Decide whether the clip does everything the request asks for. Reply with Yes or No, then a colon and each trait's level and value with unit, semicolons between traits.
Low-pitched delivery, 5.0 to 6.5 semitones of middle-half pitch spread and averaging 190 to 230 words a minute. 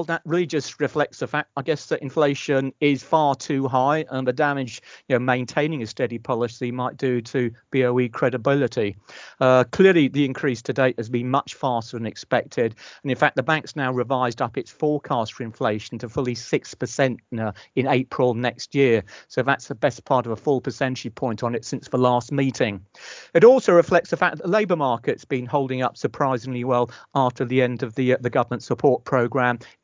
No: low, 130 Hz; average, 2.7 semitones; fast, 205 wpm